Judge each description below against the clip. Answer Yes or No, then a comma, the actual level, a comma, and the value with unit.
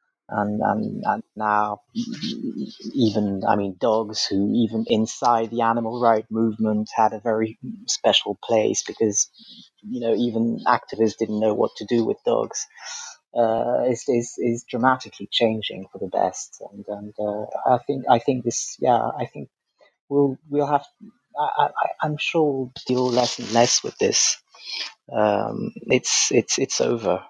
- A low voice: Yes, low, 115 Hz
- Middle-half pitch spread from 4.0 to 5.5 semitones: Yes, average, 4.6 semitones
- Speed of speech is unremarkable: Yes, average, 155 wpm